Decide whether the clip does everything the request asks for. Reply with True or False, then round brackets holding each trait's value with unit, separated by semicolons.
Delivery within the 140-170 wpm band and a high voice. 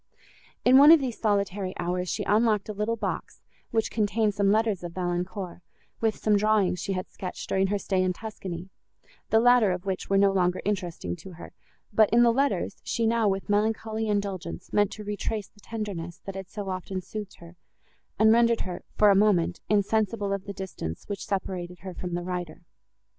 False (190 wpm; 200 Hz)